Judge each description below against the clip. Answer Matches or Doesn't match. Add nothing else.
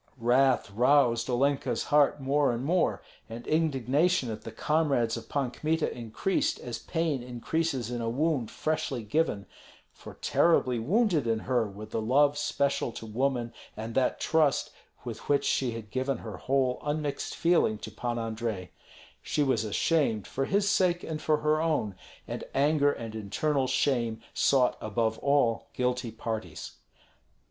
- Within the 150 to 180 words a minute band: Matches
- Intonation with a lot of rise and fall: Doesn't match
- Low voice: Matches